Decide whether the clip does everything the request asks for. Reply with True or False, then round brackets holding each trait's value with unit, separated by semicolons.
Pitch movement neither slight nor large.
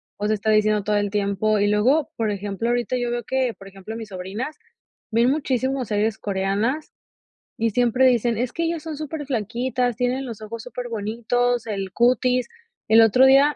True (3.4 semitones)